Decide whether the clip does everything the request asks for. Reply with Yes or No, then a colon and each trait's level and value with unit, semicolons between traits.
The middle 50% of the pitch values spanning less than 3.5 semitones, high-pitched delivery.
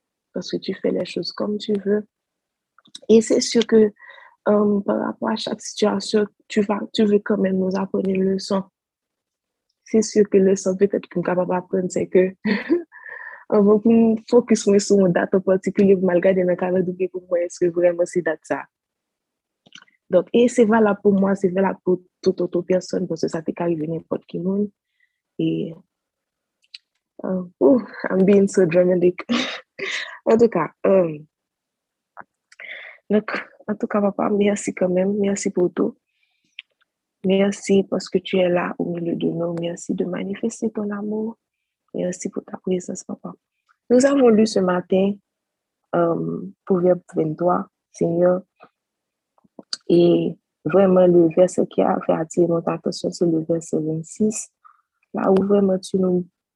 Yes: average, 2.9 semitones; high, 195 Hz